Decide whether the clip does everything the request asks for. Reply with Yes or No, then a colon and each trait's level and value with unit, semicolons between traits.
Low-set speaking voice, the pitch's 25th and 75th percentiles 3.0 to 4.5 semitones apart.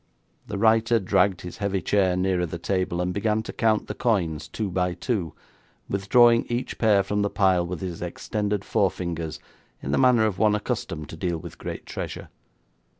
Yes: low, 100 Hz; average, 3.7 semitones